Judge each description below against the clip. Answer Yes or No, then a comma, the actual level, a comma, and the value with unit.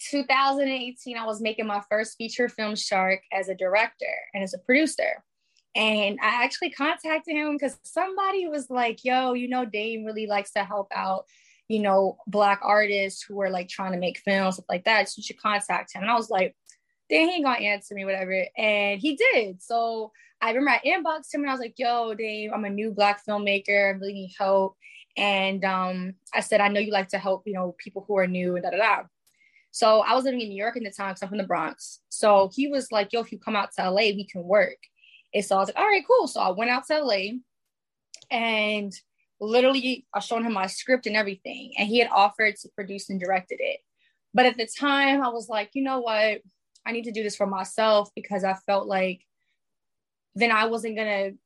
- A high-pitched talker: Yes, high, 215 Hz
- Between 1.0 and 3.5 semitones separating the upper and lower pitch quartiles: No, average, 4.2 semitones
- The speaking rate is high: Yes, fast, 225 wpm